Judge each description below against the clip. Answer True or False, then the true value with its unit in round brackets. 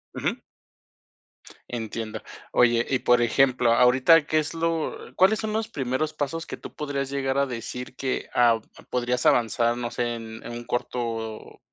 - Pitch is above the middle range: False (125 Hz)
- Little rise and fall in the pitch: False (3.2 semitones)